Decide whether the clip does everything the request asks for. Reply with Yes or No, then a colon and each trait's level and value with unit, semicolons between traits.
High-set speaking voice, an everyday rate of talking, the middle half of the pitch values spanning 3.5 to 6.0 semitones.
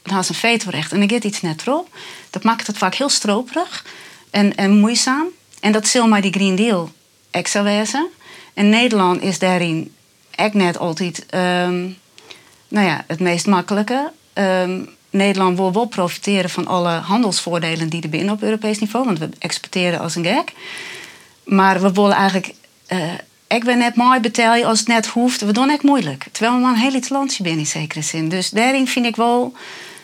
Yes: high, 205 Hz; average, 190 wpm; average, 4.8 semitones